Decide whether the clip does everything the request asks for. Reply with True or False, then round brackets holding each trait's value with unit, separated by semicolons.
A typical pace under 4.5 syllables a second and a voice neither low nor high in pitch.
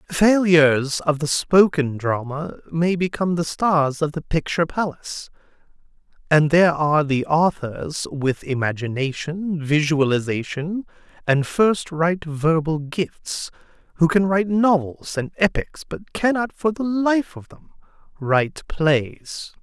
True (4.1 syllables/s; 160 Hz)